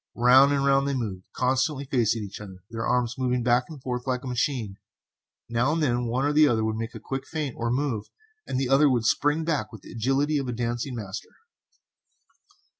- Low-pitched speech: Yes, low, 125 Hz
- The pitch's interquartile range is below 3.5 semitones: Yes, average, 3.0 semitones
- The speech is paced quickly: Yes, fast, 210 wpm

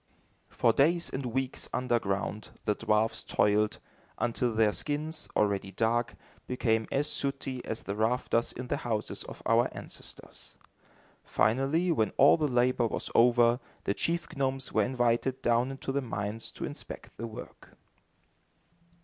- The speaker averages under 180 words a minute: Yes, average, 140 wpm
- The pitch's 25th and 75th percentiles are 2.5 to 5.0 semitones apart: Yes, average, 3.3 semitones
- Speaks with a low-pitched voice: Yes, low, 120 Hz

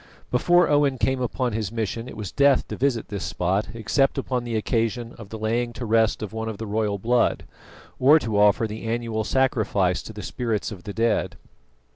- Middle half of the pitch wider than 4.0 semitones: No, narrow, 2.6 semitones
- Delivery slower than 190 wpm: No, average, 200 wpm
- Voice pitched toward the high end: No, low, 115 Hz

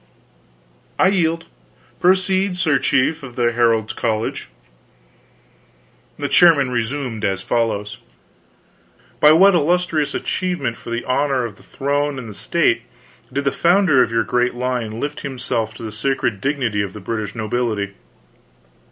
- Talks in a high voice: No, low, 125 Hz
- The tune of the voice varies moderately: Yes, average, 4.8 semitones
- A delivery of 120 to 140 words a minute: Yes, slow, 135 wpm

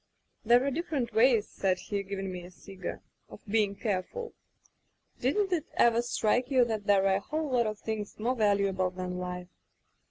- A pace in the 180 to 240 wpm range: Yes, average, 190 wpm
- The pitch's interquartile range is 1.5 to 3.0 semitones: No, average, 4.3 semitones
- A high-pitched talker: Yes, high, 215 Hz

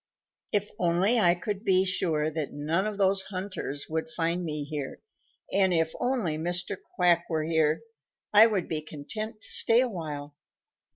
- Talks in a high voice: No, medium, 175 Hz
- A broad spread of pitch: No, average, 4.2 semitones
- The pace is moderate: Yes, average, 165 wpm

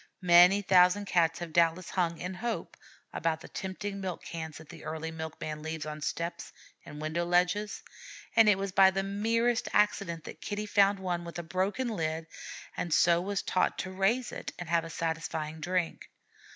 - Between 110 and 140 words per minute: No, average, 185 wpm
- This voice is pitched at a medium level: Yes, medium, 175 Hz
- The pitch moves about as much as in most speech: Yes, average, 3.3 semitones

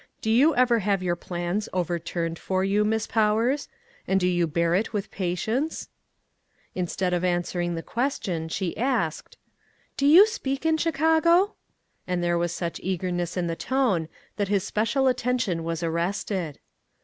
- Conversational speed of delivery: Yes, average, 170 wpm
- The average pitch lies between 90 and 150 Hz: No, high, 190 Hz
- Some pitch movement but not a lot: No, wide, 6.2 semitones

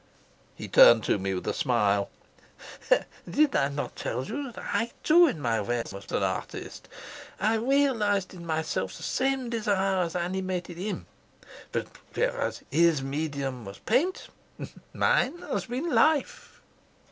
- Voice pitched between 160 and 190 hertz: Yes, medium, 185 Hz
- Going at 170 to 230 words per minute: No, average, 145 wpm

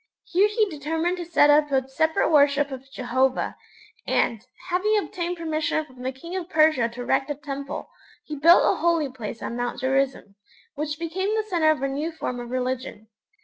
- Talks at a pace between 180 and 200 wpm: Yes, average, 190 wpm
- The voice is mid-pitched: No, very high, 295 Hz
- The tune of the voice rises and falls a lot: No, average, 4.3 semitones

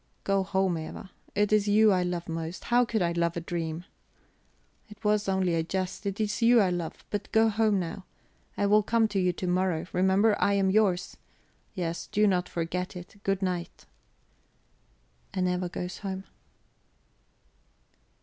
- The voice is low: No, high, 190 Hz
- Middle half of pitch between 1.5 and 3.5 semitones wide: Yes, average, 2.7 semitones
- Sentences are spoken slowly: No, average, 170 wpm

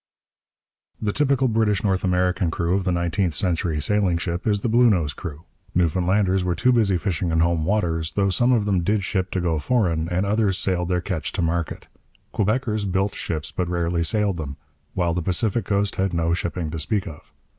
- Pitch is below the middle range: Yes, very low, 90 Hz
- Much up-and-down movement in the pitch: No, average, 3.3 semitones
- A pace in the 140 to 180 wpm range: No, average, 195 wpm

